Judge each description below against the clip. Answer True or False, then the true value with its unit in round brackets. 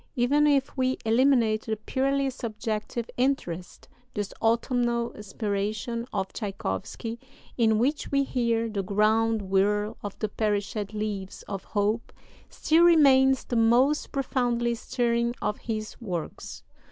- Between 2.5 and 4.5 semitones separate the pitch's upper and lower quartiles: True (3.3 semitones)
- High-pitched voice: True (230 Hz)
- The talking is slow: True (125 wpm)